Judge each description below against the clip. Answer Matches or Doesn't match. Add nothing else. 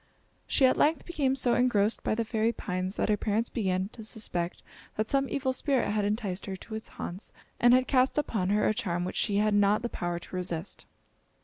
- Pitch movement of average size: Matches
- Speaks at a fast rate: Matches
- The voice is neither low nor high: Doesn't match